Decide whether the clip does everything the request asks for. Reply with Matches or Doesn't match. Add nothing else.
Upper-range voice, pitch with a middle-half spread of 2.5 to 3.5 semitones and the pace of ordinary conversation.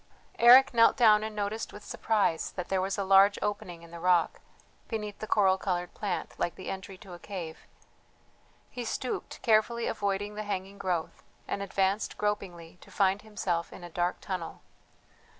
Matches